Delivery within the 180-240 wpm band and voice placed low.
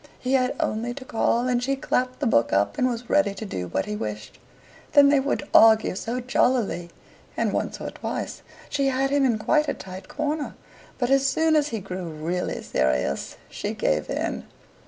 No: average, 195 wpm; high, 240 Hz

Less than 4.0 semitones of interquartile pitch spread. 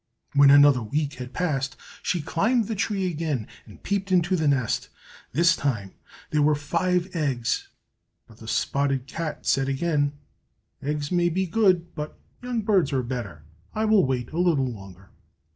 No: average, 5.1 semitones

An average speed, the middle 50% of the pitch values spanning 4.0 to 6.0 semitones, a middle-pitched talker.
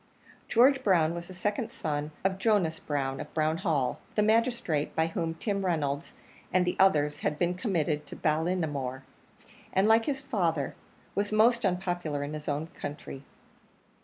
Yes: average, 160 wpm; average, 5.2 semitones; medium, 170 Hz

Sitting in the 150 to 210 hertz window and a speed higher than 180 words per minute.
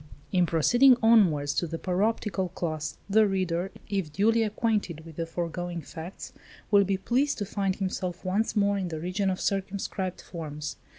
No: medium, 185 Hz; average, 165 wpm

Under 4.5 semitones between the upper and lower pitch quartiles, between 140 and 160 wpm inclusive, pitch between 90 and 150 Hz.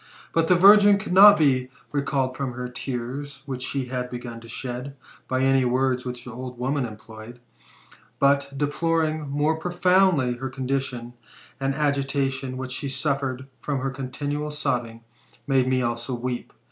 Yes: narrow, 2.5 semitones; average, 155 wpm; low, 135 Hz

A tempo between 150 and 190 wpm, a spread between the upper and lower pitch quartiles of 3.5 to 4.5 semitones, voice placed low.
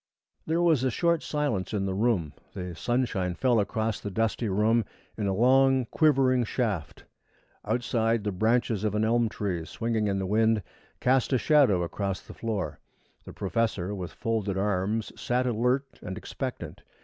Yes: average, 160 wpm; average, 4.1 semitones; low, 110 Hz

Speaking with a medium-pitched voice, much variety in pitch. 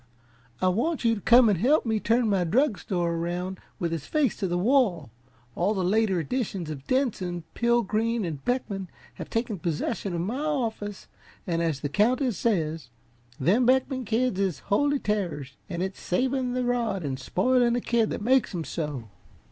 No: high, 205 Hz; wide, 5.9 semitones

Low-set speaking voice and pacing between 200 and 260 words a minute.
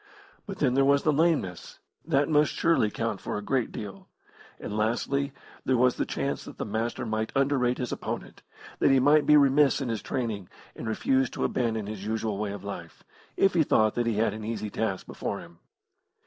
Yes: low, 120 Hz; fast, 205 wpm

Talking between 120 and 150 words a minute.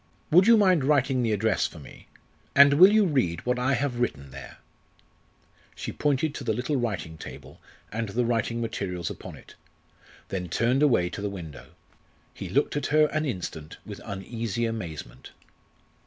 No: average, 170 wpm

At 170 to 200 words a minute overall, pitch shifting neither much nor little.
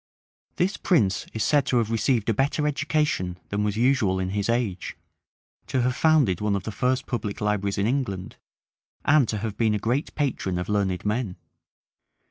Yes: average, 180 wpm; average, 4.8 semitones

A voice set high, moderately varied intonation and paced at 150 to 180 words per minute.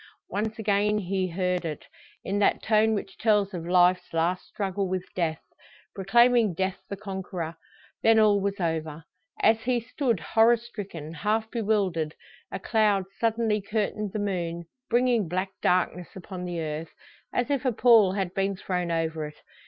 Yes: high, 195 Hz; average, 3.6 semitones; average, 160 wpm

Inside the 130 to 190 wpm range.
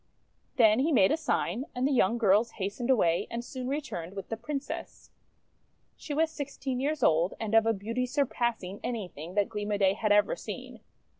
No: average, 200 wpm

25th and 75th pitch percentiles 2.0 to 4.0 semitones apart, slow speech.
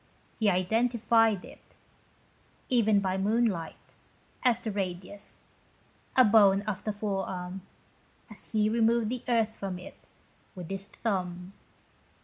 Yes: average, 2.9 semitones; slow, 120 wpm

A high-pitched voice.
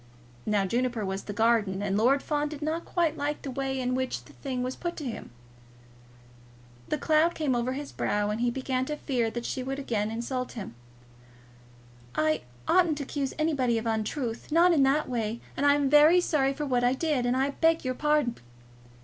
Yes: very high, 260 Hz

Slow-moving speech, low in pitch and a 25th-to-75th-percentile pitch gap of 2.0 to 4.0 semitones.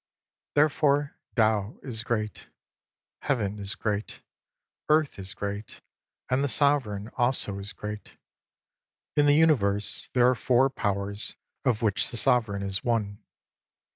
No: slow, 125 wpm; low, 110 Hz; average, 4.8 semitones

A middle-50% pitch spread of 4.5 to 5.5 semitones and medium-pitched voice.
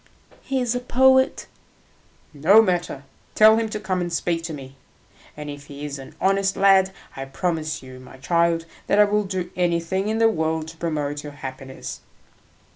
Yes: average, 5.2 semitones; medium, 170 Hz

